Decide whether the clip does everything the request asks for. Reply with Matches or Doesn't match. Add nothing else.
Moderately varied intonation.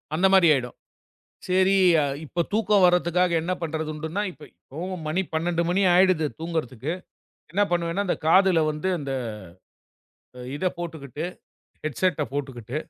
Matches